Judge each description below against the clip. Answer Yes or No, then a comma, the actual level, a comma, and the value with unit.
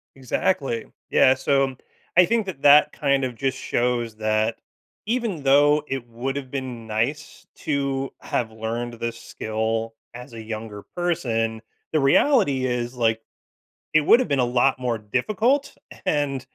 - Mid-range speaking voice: No, low, 130 Hz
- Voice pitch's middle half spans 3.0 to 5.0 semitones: Yes, average, 3.8 semitones